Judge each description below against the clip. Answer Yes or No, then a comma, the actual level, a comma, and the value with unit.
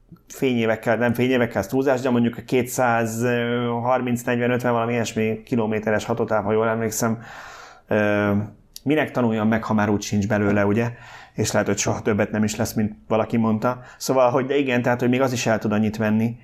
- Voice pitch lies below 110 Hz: No, low, 115 Hz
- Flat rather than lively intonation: Yes, narrow, 2.2 semitones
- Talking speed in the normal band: No, fast, 175 wpm